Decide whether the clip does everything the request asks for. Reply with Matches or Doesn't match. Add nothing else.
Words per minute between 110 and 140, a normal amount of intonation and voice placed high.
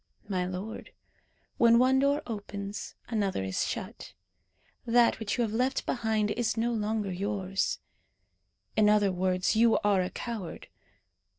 Matches